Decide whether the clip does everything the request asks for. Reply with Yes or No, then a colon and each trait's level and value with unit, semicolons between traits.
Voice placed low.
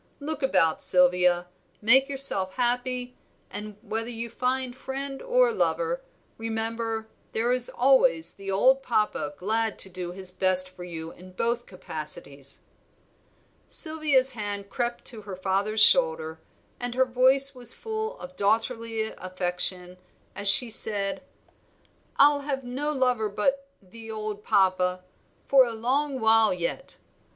No: high, 225 Hz